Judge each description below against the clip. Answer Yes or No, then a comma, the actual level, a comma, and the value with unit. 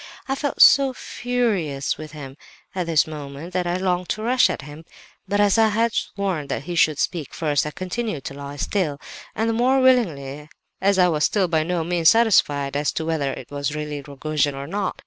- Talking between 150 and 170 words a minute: No, fast, 205 wpm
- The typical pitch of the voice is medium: Yes, medium, 165 Hz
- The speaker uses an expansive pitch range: Yes, wide, 5.9 semitones